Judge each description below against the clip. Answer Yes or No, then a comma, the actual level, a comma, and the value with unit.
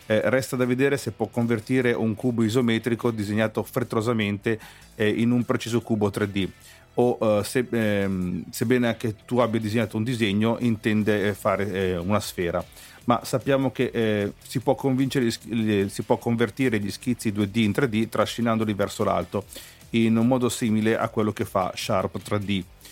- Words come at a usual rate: Yes, average, 160 wpm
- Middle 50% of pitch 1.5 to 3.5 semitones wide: Yes, average, 2.7 semitones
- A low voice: Yes, low, 115 Hz